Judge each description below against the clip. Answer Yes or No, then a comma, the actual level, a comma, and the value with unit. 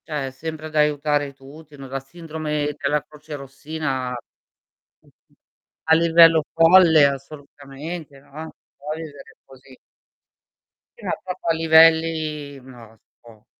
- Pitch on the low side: No, medium, 150 Hz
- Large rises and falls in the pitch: No, narrow, 2.6 semitones